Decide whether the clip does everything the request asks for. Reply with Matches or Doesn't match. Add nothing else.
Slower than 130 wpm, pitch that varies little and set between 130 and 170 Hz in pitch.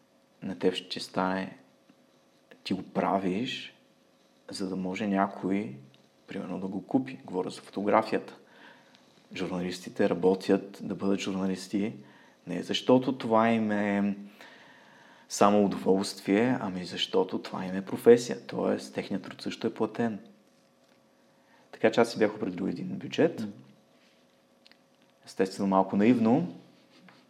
Doesn't match